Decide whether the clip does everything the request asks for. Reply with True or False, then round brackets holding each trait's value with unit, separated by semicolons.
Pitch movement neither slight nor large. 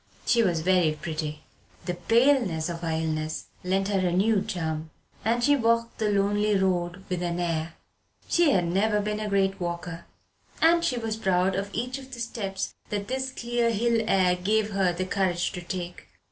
True (4.4 semitones)